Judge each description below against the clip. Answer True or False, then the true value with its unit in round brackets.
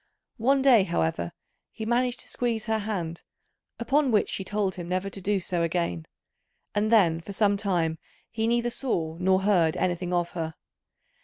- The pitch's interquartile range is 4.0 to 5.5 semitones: True (4.6 semitones)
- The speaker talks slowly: False (170 wpm)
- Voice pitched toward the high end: True (195 Hz)